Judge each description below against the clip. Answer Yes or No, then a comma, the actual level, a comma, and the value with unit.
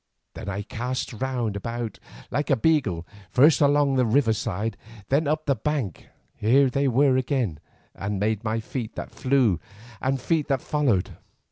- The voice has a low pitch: Yes, low, 125 Hz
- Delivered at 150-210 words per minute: Yes, average, 160 wpm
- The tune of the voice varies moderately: Yes, average, 4.3 semitones